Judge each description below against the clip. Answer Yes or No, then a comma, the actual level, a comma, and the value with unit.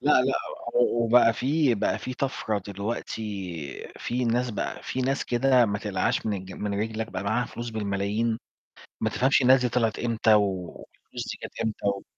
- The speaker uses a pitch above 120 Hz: No, low, 115 Hz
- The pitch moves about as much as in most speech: Yes, average, 3.2 semitones